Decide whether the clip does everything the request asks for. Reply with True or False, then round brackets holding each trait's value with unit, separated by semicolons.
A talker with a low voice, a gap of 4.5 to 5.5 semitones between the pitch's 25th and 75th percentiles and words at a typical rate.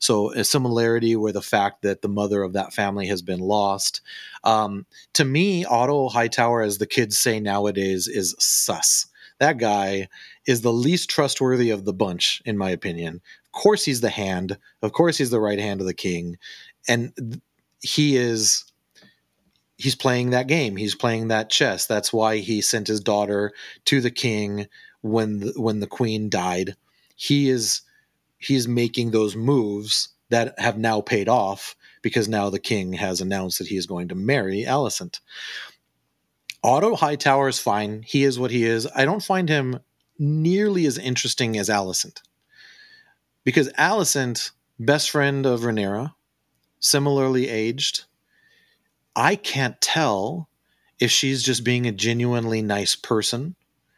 True (115 Hz; 4.8 semitones; 155 wpm)